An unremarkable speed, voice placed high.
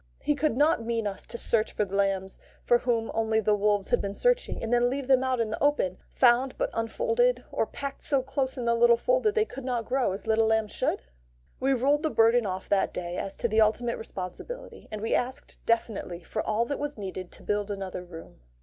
No: fast, 230 wpm; high, 230 Hz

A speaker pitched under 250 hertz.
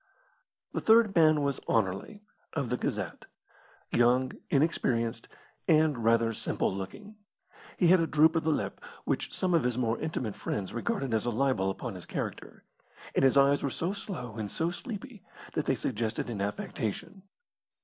Yes: low, 135 Hz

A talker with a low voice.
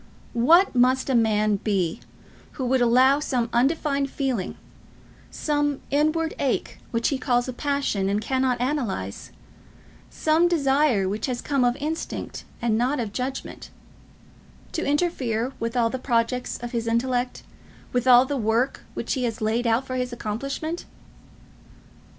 No: very high, 250 Hz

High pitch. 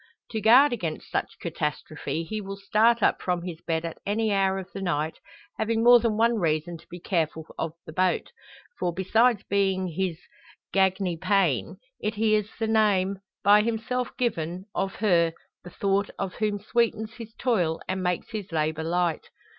Yes: high, 195 Hz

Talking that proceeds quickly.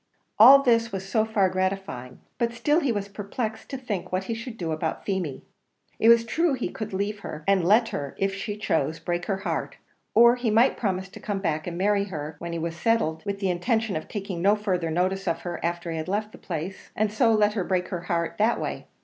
Yes: fast, 235 wpm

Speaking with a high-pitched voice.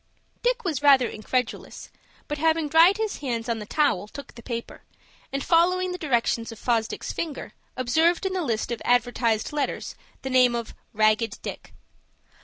Yes: very high, 255 Hz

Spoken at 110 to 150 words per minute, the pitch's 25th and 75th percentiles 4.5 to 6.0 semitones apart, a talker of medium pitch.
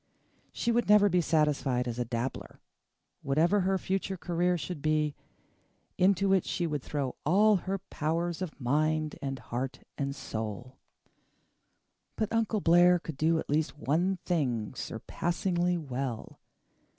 Yes: average, 140 wpm; average, 4.9 semitones; medium, 160 Hz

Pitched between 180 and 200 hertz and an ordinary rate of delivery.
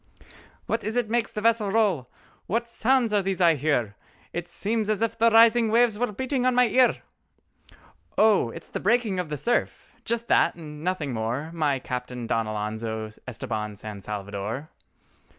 Yes: medium, 185 Hz; average, 170 wpm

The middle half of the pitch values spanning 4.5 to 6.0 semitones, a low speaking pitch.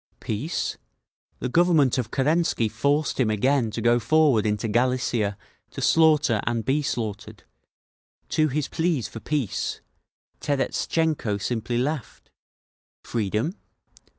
Yes: average, 5.2 semitones; low, 125 Hz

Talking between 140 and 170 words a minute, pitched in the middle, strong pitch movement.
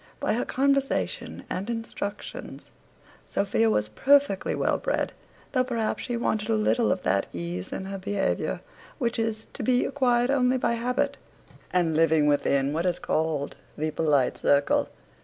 No: average, 155 wpm; high, 210 Hz; wide, 7.5 semitones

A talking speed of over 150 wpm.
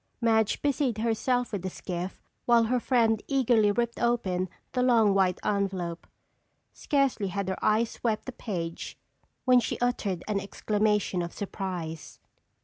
No: average, 145 wpm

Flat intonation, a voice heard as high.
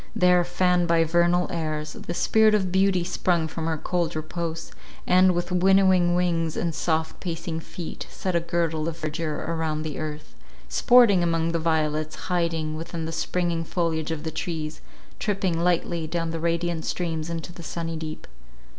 No: narrow, 1.7 semitones; medium, 170 Hz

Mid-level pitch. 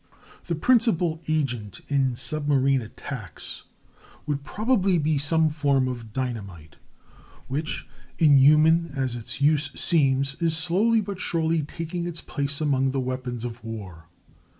Yes: medium, 145 Hz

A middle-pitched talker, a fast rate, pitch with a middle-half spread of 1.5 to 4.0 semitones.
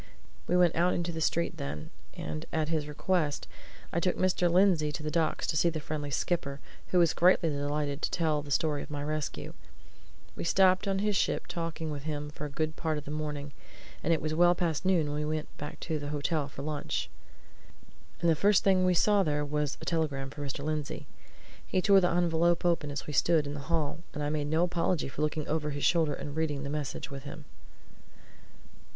Yes: medium, 155 Hz; fast, 215 wpm; average, 2.7 semitones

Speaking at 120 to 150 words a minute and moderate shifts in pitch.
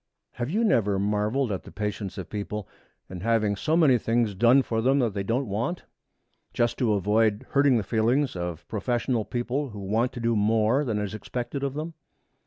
No: average, 195 wpm; average, 3.6 semitones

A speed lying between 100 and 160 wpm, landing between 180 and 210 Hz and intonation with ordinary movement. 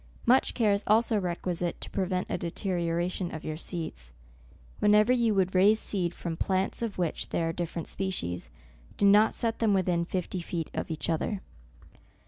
No: average, 170 wpm; medium, 185 Hz; average, 3.4 semitones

